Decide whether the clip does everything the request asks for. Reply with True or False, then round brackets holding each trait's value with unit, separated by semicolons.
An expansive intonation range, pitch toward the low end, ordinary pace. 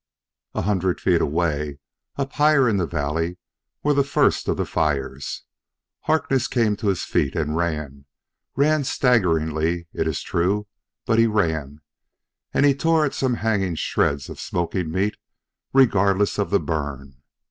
True (7.2 semitones; 90 Hz; 150 wpm)